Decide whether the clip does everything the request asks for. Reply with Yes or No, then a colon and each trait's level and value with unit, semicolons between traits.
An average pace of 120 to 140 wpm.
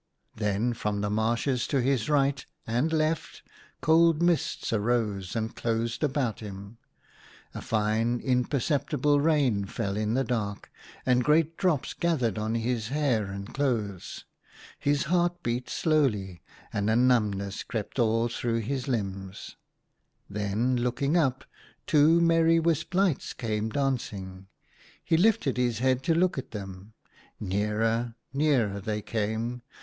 Yes: slow, 135 wpm